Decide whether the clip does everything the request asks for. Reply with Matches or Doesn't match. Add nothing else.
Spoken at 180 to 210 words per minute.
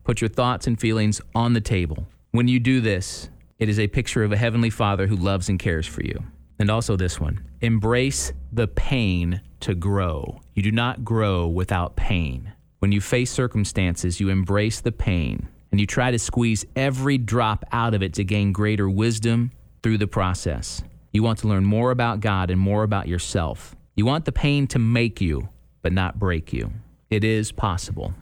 Matches